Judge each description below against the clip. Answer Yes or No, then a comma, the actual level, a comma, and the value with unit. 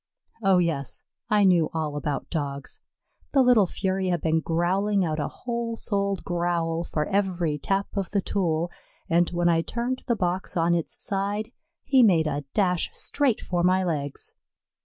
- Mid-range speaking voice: Yes, medium, 180 Hz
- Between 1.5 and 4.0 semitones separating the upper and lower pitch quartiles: Yes, average, 3.4 semitones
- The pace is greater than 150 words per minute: Yes, average, 165 wpm